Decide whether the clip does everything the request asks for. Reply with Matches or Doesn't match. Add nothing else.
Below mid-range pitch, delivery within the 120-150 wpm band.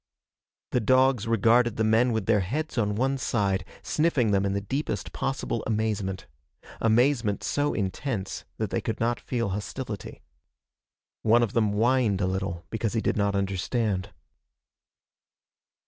Matches